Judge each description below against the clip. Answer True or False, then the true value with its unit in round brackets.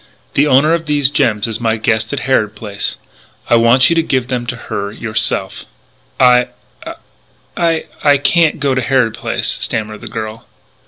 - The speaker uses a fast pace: False (165 wpm)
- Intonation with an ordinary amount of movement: True (4.3 semitones)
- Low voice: True (125 Hz)